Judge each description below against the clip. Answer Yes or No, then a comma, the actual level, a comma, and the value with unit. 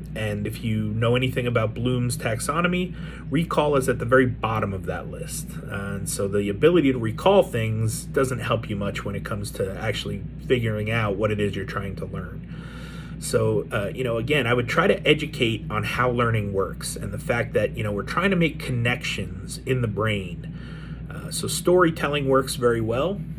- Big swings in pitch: Yes, wide, 5.9 semitones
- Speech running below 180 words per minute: No, average, 195 wpm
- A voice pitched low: Yes, low, 125 Hz